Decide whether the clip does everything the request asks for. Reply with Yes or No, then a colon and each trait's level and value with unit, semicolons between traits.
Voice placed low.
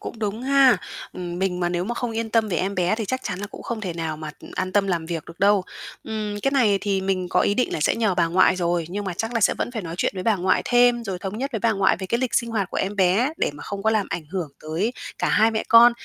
No: high, 200 Hz